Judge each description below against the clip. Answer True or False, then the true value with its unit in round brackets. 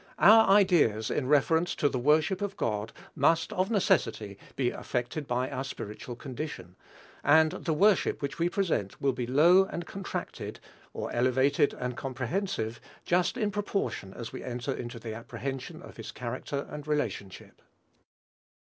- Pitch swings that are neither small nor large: False (6.1 semitones)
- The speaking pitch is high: False (140 Hz)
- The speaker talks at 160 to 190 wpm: False (150 wpm)